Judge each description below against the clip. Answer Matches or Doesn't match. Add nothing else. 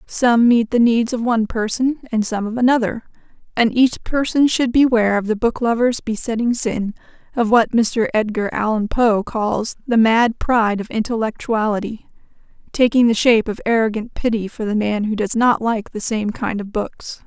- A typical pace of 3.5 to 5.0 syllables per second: Matches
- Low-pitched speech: Doesn't match